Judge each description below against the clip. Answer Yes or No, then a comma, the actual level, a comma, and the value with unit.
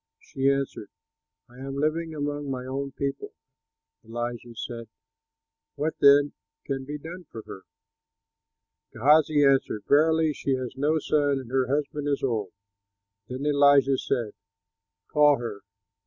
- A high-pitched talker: No, medium, 140 Hz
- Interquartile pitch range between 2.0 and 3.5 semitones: Yes, narrow, 2.5 semitones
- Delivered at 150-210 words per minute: No, slow, 135 wpm